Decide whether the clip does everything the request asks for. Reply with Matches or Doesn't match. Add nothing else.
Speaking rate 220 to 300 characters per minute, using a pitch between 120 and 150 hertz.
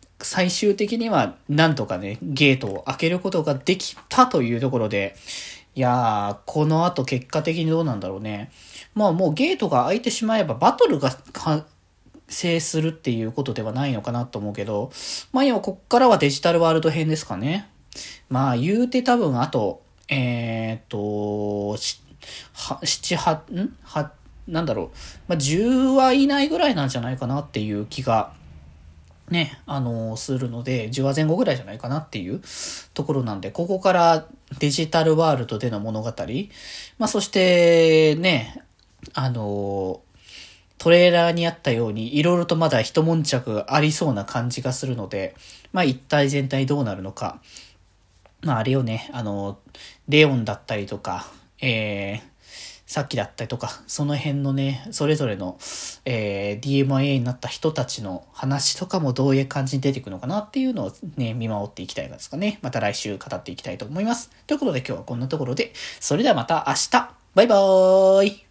Doesn't match